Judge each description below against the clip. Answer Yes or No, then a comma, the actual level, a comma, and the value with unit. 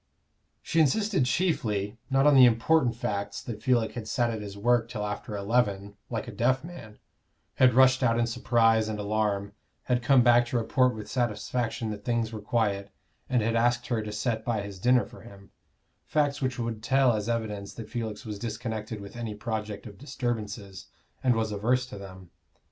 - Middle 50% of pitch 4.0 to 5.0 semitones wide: No, average, 2.8 semitones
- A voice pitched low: Yes, low, 115 Hz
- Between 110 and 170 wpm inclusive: No, average, 190 wpm